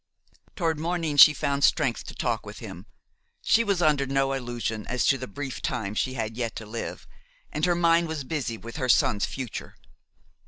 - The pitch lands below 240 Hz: Yes, low, 135 Hz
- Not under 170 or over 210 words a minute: Yes, average, 190 wpm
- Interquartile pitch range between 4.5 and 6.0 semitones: Yes, average, 5.0 semitones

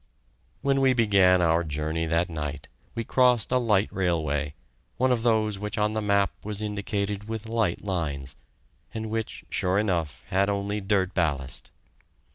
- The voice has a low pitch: Yes, low, 100 Hz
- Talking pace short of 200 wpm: Yes, average, 155 wpm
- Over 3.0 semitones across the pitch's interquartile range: Yes, average, 4.5 semitones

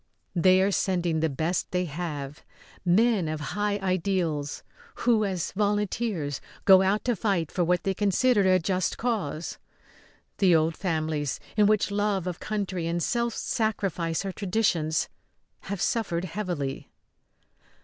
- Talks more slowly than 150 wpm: Yes, average, 140 wpm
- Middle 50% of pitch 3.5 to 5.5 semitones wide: Yes, average, 3.9 semitones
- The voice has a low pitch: No, medium, 185 Hz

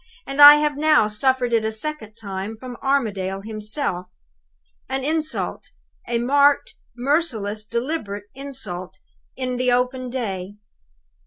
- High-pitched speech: Yes, high, 245 Hz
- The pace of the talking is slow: Yes, slow, 120 wpm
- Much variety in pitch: No, average, 4.9 semitones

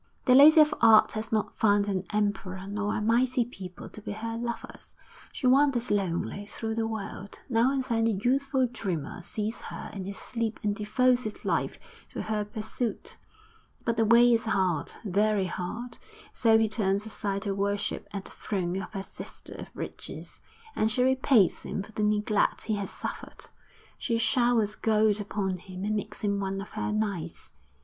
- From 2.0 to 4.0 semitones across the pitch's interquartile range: Yes, narrow, 2.6 semitones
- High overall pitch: Yes, high, 215 Hz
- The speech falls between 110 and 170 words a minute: No, average, 180 wpm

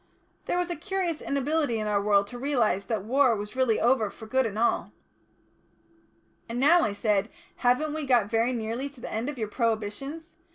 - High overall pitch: Yes, high, 240 Hz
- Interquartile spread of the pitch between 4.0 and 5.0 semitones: Yes, average, 4.7 semitones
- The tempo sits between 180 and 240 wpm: Yes, average, 195 wpm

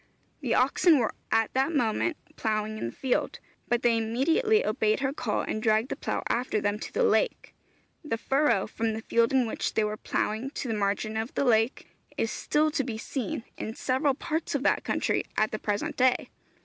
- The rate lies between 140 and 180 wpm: No, average, 200 wpm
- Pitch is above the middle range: Yes, high, 230 Hz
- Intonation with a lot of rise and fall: No, average, 3.9 semitones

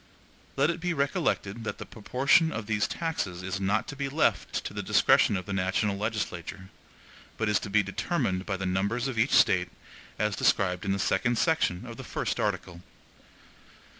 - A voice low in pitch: Yes, low, 105 Hz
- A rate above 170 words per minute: Yes, average, 185 wpm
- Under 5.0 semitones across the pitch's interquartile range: No, average, 5.3 semitones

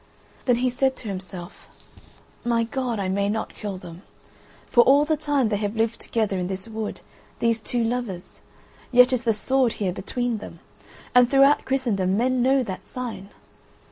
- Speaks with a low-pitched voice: No, high, 230 Hz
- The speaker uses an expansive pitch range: No, average, 4.0 semitones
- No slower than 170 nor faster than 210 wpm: Yes, average, 175 wpm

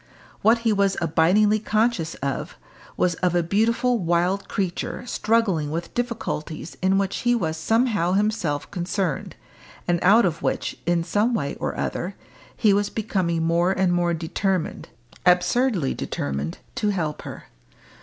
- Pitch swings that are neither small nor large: Yes, average, 4.2 semitones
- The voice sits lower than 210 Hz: Yes, medium, 185 Hz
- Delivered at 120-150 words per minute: Yes, average, 145 wpm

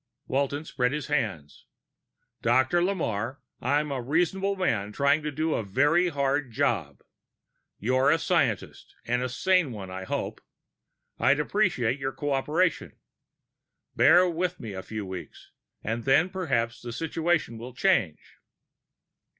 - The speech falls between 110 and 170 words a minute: Yes, slow, 135 wpm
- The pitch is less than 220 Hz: Yes, medium, 140 Hz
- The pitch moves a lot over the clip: Yes, wide, 5.8 semitones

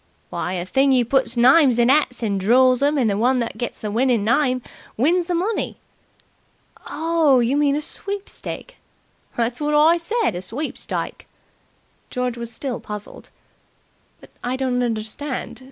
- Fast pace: No, average, 155 wpm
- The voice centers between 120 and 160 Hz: No, very high, 255 Hz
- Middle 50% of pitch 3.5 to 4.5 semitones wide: Yes, average, 4.1 semitones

